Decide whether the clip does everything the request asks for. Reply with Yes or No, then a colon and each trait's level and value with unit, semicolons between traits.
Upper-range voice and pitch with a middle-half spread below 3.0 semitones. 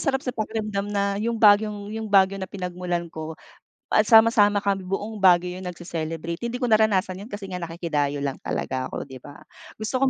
No: high, 200 Hz; average, 3.8 semitones